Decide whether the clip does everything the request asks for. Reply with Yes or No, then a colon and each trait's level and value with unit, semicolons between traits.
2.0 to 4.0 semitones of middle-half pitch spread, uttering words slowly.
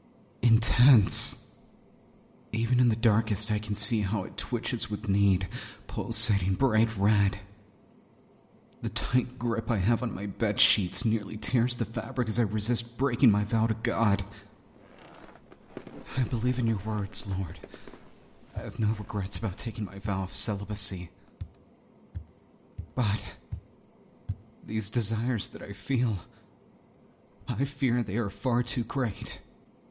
Yes: average, 2.8 semitones; slow, 130 wpm